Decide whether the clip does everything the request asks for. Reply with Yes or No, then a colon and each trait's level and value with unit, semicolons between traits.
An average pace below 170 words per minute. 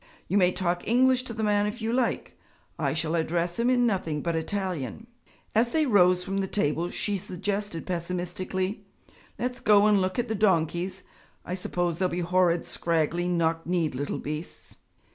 No: average, 175 wpm